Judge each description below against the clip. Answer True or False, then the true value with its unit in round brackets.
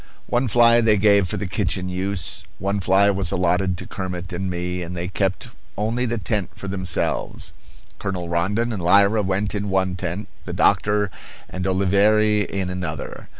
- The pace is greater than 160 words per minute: True (170 wpm)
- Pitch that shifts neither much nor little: False (2.2 semitones)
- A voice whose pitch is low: True (95 Hz)